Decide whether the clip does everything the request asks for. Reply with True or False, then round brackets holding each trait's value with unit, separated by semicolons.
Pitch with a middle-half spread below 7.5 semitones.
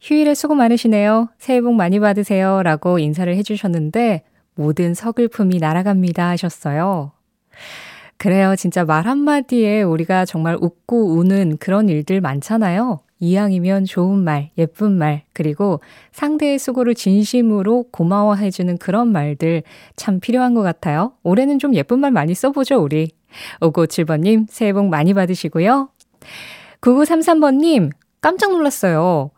True (5.4 semitones)